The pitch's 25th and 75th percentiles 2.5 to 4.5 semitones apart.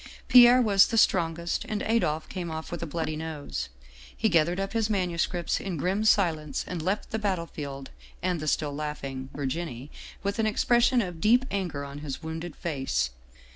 No: average, 4.9 semitones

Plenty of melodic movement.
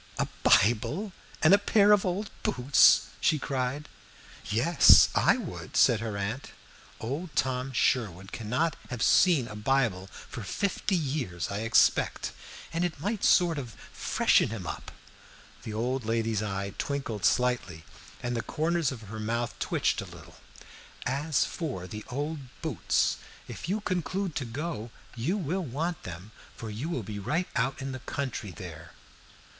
Yes: wide, 6.8 semitones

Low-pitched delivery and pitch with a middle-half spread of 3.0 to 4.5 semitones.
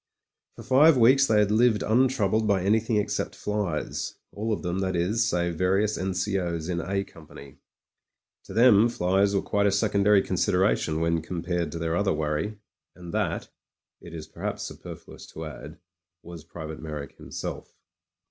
Yes: very low, 95 Hz; average, 4.0 semitones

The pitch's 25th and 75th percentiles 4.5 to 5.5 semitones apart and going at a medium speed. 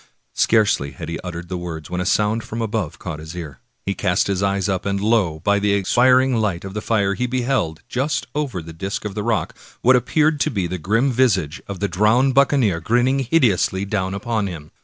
No: average, 5.0 semitones; fast, 215 wpm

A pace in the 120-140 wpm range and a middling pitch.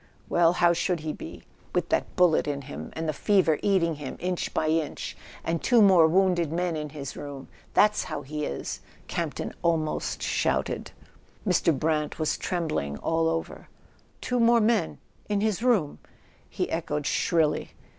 No: average, 170 wpm; medium, 165 Hz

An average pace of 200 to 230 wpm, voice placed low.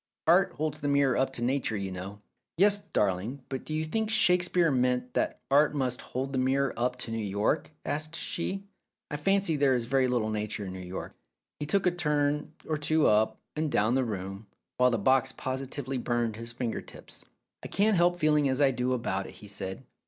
Yes: fast, 205 wpm; low, 130 Hz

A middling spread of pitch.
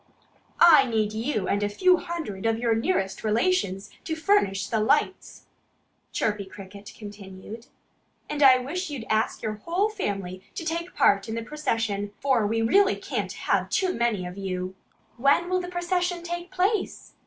No: wide, 9.0 semitones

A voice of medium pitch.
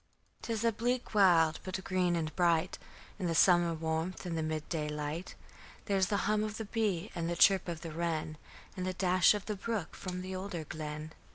Yes: medium, 180 Hz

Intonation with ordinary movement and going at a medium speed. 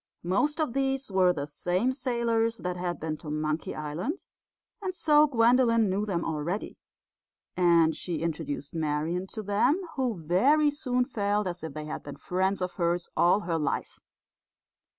No: wide, 6.7 semitones; average, 160 wpm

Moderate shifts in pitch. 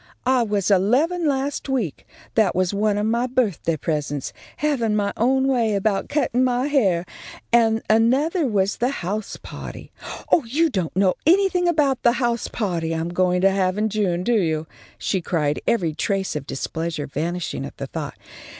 No: wide, 6.0 semitones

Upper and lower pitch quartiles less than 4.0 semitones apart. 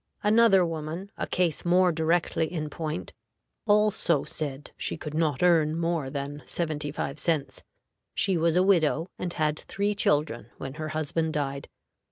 Yes: average, 2.8 semitones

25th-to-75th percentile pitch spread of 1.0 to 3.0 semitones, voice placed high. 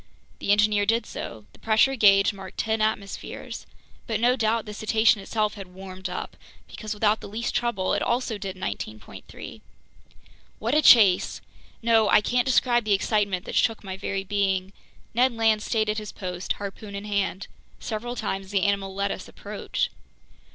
Yes: narrow, 2.4 semitones; high, 210 Hz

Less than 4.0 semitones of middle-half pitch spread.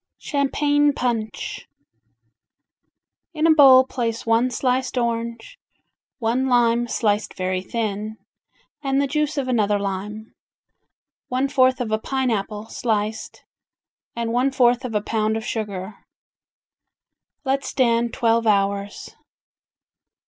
Yes: average, 3.3 semitones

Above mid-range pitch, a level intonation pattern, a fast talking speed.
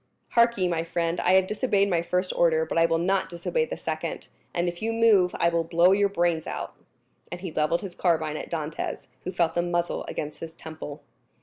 No: medium, 175 Hz; narrow, 2.3 semitones; fast, 215 wpm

